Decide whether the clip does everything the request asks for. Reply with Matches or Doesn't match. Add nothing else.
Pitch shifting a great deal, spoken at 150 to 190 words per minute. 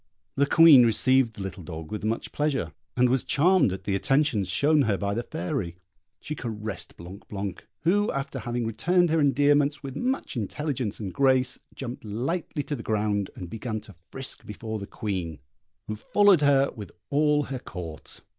Matches